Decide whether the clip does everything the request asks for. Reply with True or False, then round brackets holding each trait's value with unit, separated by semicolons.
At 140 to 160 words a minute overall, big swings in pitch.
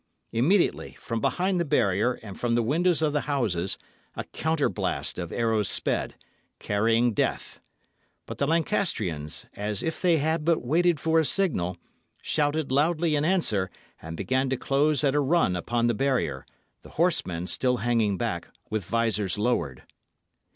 True (155 wpm; 7.1 semitones)